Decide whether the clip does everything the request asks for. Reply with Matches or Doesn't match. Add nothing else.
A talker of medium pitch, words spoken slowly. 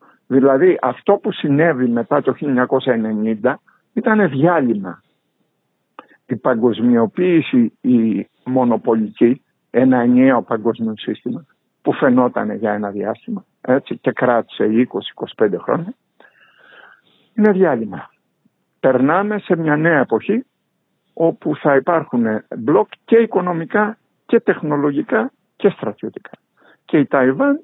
Matches